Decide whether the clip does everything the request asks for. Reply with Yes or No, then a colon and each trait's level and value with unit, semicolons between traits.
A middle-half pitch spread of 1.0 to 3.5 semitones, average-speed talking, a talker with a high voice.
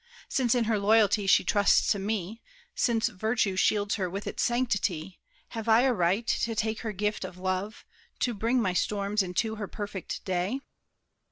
Yes: average, 2.7 semitones; average, 175 wpm; high, 210 Hz